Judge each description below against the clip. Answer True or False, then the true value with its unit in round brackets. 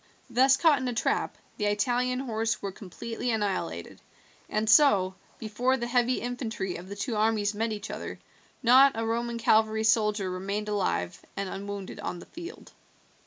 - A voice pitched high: True (220 Hz)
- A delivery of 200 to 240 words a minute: False (165 wpm)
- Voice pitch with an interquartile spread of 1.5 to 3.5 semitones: True (3.2 semitones)